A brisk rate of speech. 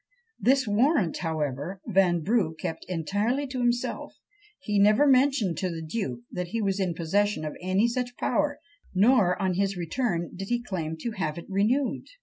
No: average, 165 wpm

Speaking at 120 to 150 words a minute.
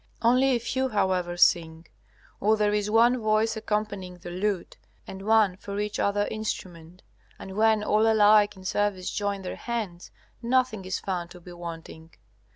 No: average, 165 wpm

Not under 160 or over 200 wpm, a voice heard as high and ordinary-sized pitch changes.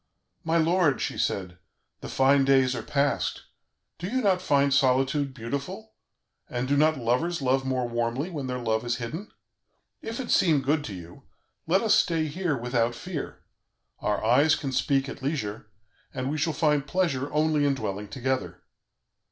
No: average, 170 wpm; medium, 140 Hz; average, 4.1 semitones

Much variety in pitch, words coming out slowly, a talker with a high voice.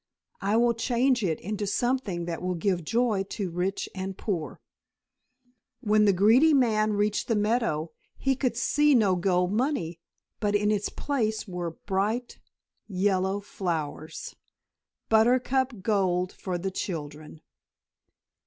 No: average, 4.3 semitones; slow, 130 wpm; high, 205 Hz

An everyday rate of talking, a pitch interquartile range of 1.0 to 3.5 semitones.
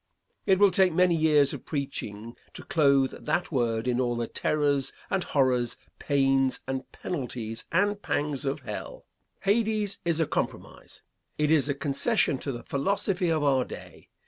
No: average, 160 wpm; average, 5.1 semitones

